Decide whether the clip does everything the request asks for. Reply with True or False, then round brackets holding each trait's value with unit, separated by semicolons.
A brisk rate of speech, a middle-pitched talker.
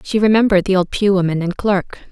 False (225 wpm; 195 Hz)